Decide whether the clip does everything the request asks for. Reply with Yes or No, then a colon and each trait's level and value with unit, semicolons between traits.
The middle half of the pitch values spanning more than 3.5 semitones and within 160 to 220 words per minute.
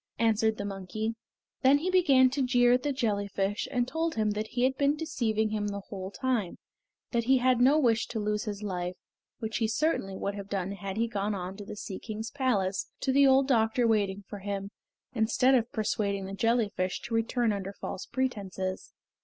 Yes: average, 3.9 semitones; average, 200 wpm